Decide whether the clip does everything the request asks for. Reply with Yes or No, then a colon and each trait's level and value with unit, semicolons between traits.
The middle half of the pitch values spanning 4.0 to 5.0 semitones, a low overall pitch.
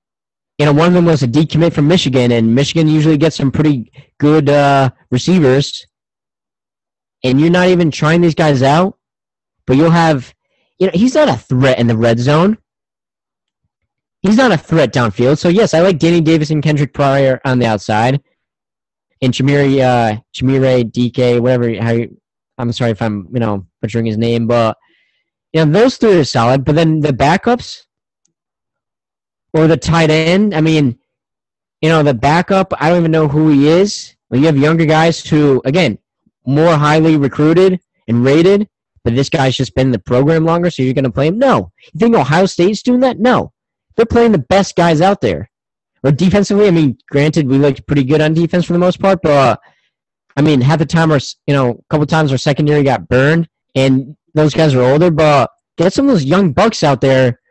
No: average, 4.4 semitones; medium, 150 Hz